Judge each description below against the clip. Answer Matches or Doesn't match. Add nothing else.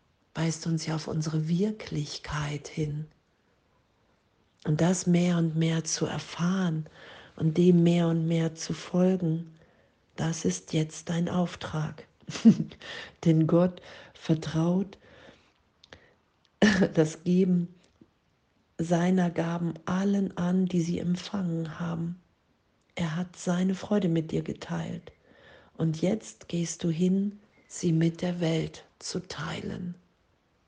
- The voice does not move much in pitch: Matches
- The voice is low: Doesn't match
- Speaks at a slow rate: Matches